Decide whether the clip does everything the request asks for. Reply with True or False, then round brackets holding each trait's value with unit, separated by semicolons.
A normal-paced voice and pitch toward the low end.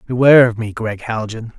True (190 wpm; 115 Hz)